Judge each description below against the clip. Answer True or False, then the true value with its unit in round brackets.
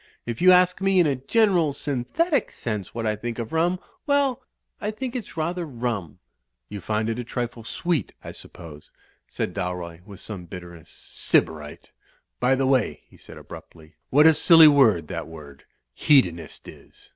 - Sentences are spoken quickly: False (170 wpm)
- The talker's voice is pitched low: True (125 Hz)